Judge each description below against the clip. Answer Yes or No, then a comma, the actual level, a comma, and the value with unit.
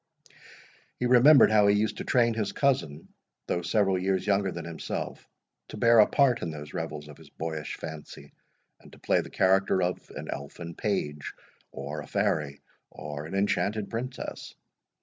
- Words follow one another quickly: No, average, 170 wpm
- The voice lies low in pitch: Yes, very low, 95 Hz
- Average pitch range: No, wide, 5.9 semitones